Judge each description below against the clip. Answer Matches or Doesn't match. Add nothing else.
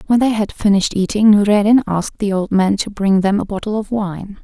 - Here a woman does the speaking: Matches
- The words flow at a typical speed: Doesn't match